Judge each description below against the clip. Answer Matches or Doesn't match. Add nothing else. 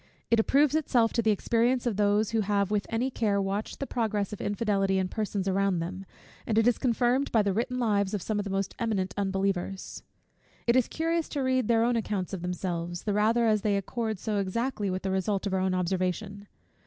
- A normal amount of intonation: Matches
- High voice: Matches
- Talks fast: Matches